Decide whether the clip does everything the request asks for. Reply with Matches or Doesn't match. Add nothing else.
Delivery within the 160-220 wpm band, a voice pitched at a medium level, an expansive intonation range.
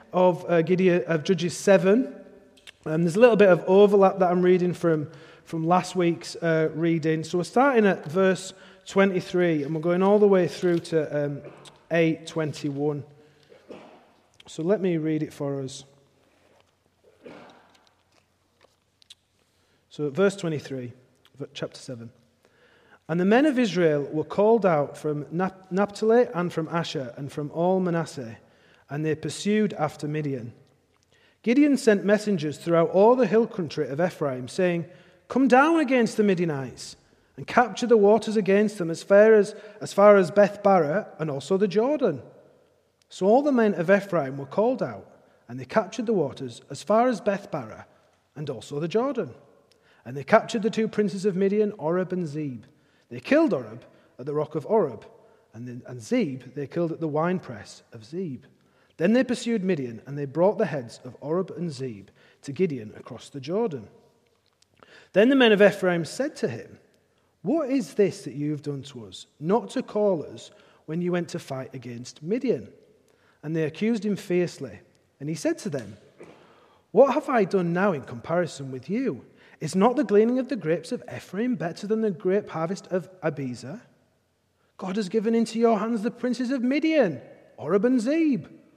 Matches